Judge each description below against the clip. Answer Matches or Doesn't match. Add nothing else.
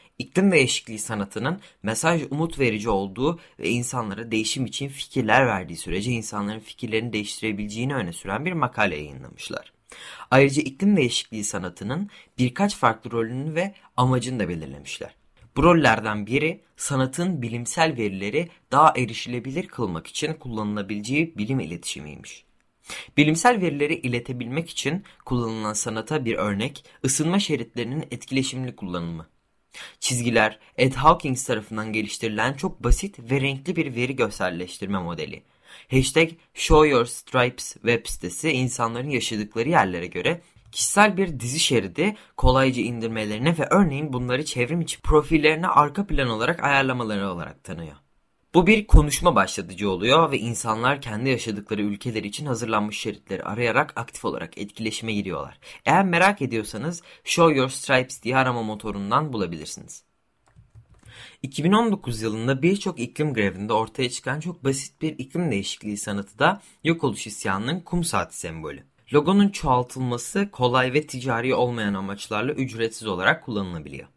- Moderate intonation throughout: Doesn't match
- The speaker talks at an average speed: Matches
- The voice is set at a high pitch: Doesn't match